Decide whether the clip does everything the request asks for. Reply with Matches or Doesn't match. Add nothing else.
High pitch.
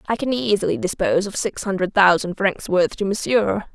Matches